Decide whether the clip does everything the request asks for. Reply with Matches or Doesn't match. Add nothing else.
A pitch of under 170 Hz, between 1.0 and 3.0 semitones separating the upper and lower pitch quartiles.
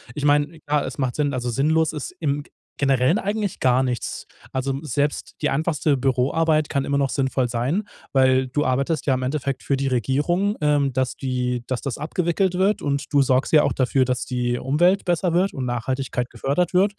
Doesn't match